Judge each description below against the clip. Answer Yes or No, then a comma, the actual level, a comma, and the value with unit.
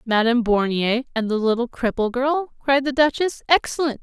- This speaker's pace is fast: No, average, 165 wpm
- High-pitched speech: Yes, very high, 250 Hz